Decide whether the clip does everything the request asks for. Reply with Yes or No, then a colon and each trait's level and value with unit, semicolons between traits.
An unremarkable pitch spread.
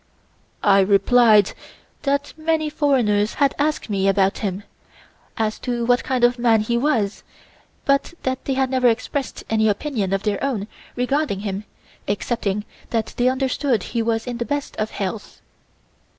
Yes: average, 4.4 semitones